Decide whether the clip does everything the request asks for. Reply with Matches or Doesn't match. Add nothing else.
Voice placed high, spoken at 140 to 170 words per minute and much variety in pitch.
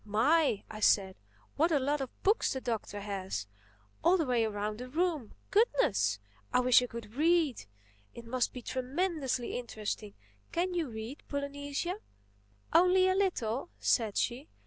Matches